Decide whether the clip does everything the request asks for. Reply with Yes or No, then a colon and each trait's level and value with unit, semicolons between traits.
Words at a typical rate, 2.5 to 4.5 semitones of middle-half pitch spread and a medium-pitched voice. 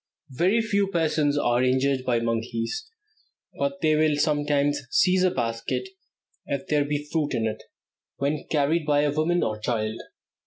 Yes: average, 155 wpm; average, 4.0 semitones; medium, 145 Hz